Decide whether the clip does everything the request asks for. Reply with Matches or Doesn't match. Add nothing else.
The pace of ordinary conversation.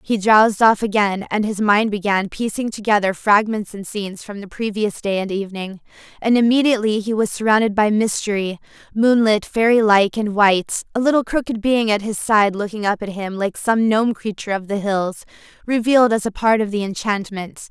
Matches